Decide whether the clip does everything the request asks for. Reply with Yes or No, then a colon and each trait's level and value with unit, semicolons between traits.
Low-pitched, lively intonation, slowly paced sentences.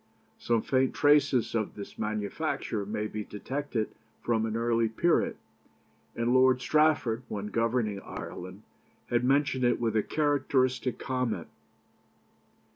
No: low, 120 Hz; average, 3.2 semitones; slow, 120 wpm